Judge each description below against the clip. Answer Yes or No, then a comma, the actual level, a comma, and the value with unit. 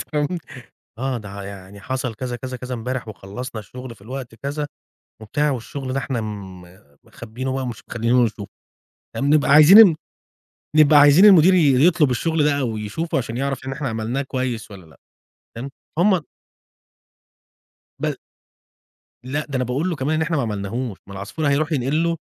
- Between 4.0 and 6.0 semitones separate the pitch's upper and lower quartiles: Yes, average, 4.7 semitones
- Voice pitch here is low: Yes, low, 130 Hz